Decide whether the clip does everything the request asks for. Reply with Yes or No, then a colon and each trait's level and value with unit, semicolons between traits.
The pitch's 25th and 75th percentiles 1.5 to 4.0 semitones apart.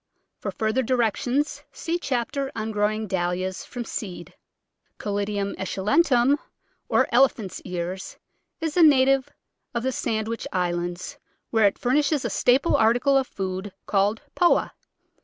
No: wide, 5.5 semitones